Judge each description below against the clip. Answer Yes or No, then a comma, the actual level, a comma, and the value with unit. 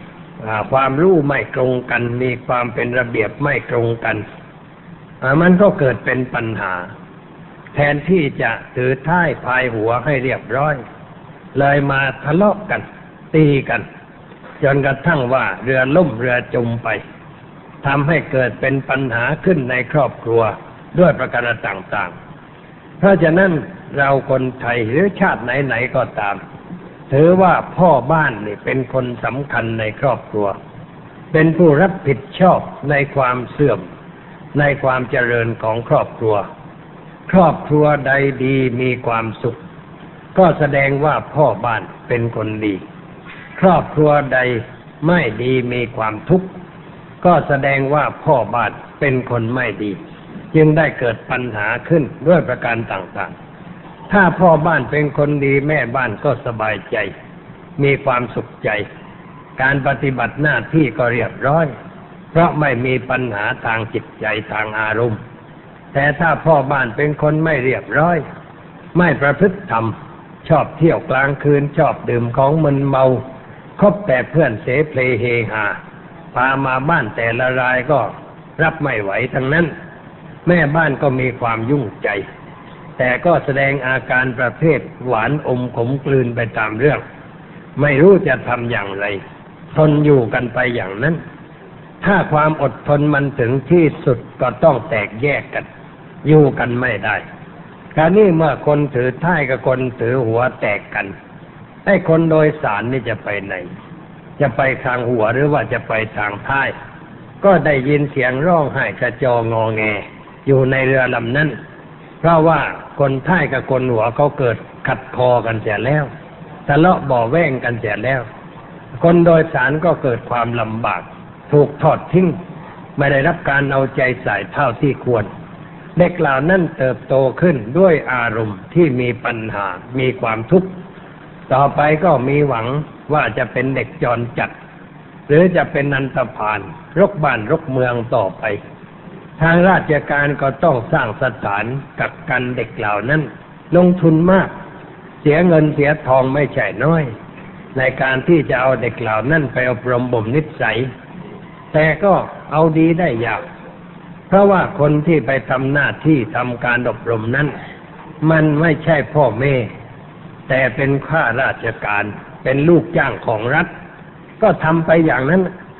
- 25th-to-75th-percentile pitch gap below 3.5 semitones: No, average, 4.7 semitones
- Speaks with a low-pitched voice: No, medium, 145 Hz